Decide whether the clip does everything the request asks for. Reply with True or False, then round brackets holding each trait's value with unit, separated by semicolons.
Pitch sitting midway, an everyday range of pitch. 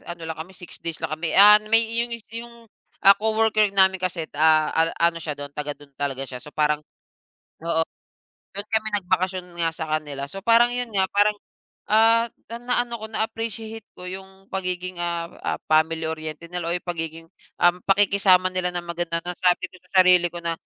True (180 Hz; 4.4 semitones)